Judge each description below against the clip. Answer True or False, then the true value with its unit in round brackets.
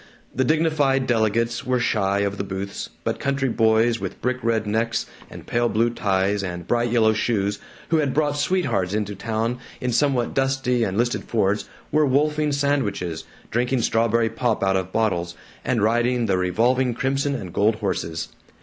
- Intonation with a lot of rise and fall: False (4.2 semitones)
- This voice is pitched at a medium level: False (115 Hz)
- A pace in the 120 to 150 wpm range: False (165 wpm)